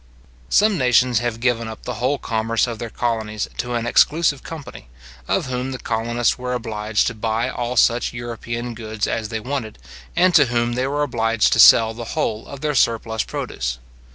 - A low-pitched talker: Yes, low, 120 Hz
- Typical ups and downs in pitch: No, narrow, 2.0 semitones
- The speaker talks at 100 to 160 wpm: No, average, 185 wpm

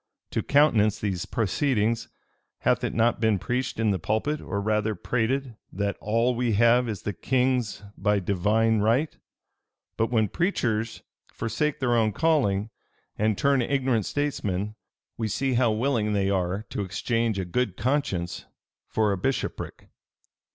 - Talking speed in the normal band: Yes, average, 145 wpm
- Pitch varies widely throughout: No, average, 3.4 semitones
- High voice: No, low, 110 Hz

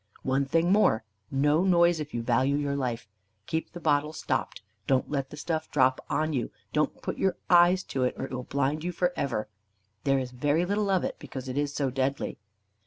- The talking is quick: Yes, fast, 210 wpm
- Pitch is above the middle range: No, medium, 145 Hz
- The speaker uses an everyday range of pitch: Yes, average, 3.8 semitones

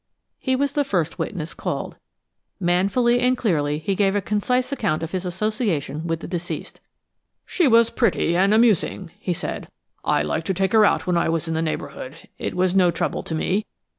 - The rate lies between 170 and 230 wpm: Yes, average, 195 wpm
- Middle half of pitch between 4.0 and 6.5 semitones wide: Yes, average, 4.9 semitones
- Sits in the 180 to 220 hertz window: Yes, medium, 185 Hz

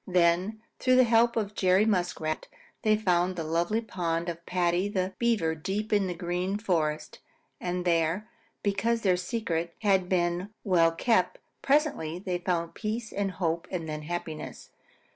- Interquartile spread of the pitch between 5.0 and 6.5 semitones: No, average, 3.7 semitones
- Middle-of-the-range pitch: Yes, medium, 180 Hz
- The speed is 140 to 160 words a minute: Yes, average, 155 wpm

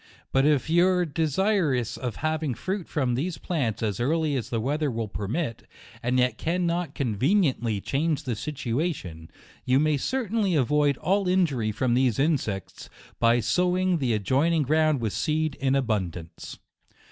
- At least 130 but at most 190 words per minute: Yes, average, 155 wpm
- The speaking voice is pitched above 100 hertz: Yes, medium, 140 Hz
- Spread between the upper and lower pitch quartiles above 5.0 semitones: Yes, wide, 5.6 semitones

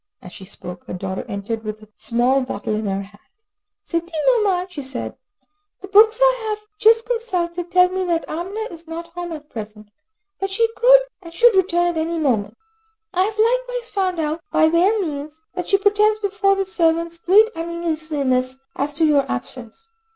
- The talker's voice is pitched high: Yes, very high, 335 Hz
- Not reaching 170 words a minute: No, average, 175 wpm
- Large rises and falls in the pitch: Yes, wide, 6.5 semitones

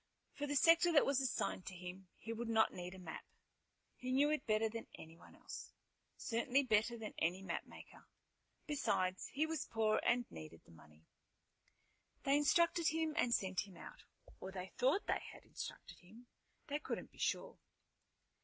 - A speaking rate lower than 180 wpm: Yes, average, 170 wpm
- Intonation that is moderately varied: No, wide, 7.3 semitones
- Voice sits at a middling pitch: No, high, 225 Hz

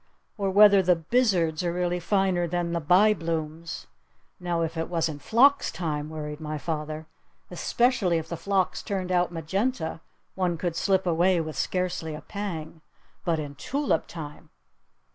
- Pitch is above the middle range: No, medium, 170 Hz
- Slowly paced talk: No, average, 155 wpm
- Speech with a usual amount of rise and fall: Yes, average, 3.1 semitones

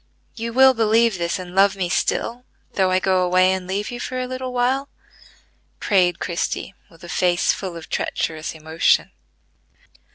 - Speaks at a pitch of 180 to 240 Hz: Yes, high, 190 Hz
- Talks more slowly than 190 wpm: Yes, average, 165 wpm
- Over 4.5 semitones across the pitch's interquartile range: Yes, average, 4.9 semitones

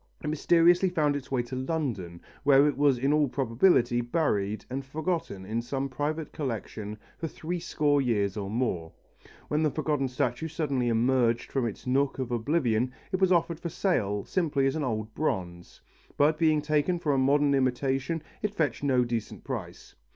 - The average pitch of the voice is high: No, low, 135 Hz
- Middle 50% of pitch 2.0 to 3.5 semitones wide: No, average, 4.5 semitones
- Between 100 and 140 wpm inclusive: No, average, 175 wpm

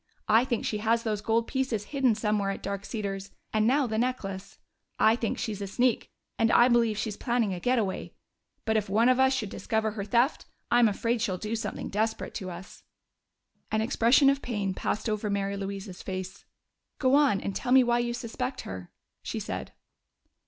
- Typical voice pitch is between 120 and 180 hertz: No, high, 220 Hz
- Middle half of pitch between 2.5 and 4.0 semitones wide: Yes, average, 3.2 semitones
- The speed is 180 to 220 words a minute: Yes, average, 190 wpm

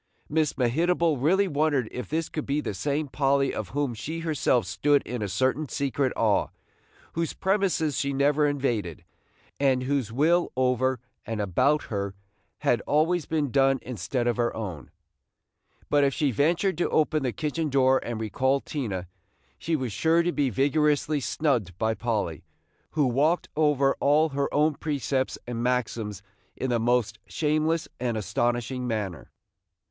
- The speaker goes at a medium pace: Yes, average, 155 wpm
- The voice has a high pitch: No, low, 135 Hz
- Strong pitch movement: No, average, 4.1 semitones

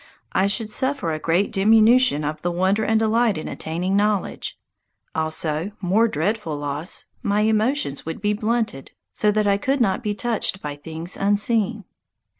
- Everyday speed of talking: Yes, average, 160 wpm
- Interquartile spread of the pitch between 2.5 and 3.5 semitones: No, average, 5.1 semitones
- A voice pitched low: No, high, 205 Hz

